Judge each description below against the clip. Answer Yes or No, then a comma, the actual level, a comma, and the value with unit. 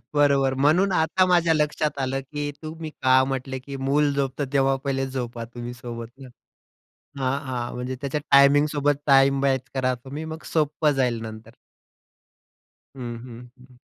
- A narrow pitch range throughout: Yes, narrow, 2.3 semitones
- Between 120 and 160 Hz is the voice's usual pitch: Yes, low, 135 Hz